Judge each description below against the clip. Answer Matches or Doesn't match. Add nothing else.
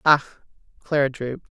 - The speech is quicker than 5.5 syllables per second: Doesn't match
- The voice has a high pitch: Doesn't match